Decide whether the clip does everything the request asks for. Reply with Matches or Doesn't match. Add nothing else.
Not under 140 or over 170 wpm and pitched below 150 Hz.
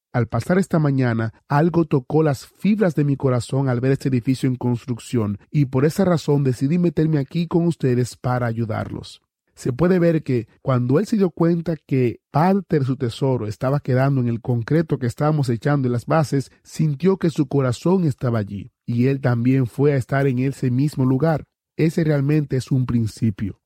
Doesn't match